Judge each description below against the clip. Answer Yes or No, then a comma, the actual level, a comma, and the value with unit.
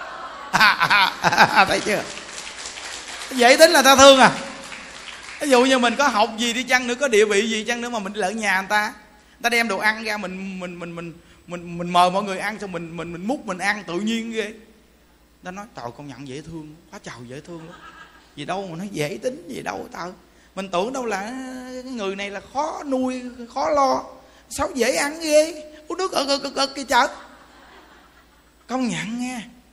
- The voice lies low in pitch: No, high, 220 Hz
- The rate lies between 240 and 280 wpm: No, average, 210 wpm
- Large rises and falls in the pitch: Yes, wide, 6.1 semitones